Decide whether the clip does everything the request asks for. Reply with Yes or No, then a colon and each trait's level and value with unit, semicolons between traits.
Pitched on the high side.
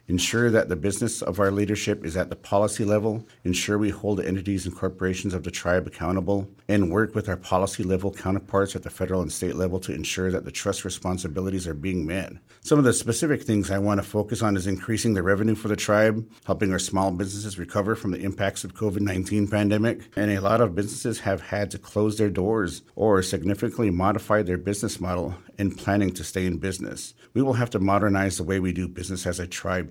No: low, 100 Hz